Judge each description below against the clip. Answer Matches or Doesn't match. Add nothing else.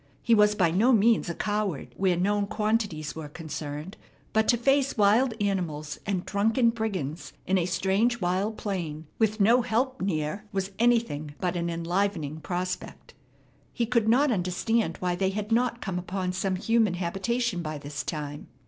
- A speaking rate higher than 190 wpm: Doesn't match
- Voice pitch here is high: Matches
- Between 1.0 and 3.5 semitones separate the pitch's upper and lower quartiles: Doesn't match